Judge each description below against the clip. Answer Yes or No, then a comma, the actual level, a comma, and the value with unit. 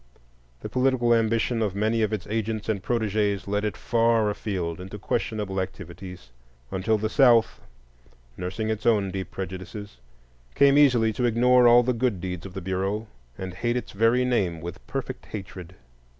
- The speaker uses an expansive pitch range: No, average, 3.6 semitones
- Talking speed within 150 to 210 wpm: Yes, average, 165 wpm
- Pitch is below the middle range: Yes, low, 110 Hz